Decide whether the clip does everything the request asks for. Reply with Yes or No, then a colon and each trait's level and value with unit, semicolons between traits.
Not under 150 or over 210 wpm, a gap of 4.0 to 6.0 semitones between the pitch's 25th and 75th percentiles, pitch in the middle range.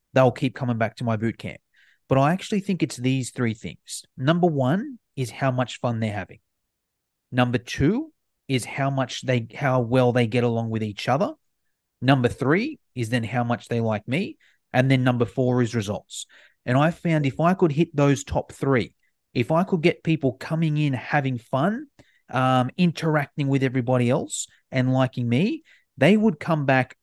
No: average, 185 wpm; average, 4.3 semitones; low, 130 Hz